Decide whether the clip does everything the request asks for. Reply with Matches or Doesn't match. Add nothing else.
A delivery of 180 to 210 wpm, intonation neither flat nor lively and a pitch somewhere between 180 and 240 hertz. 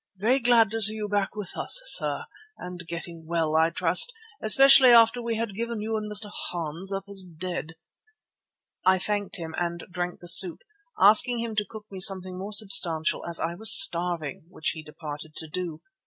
Matches